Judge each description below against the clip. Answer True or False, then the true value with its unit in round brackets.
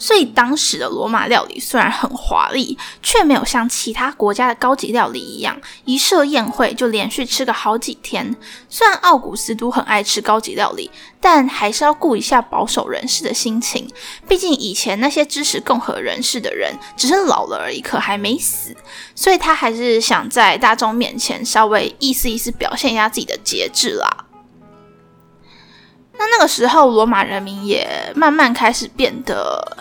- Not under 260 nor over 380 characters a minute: True (270 characters per minute)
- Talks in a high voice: True (250 Hz)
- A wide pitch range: False (4.6 semitones)